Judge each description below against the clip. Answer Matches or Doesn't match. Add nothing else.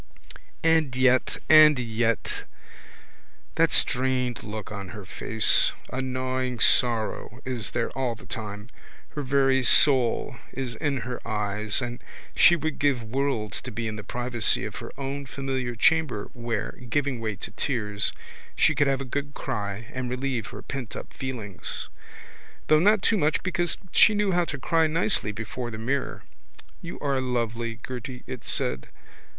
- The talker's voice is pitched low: Matches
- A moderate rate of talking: Matches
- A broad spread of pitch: Doesn't match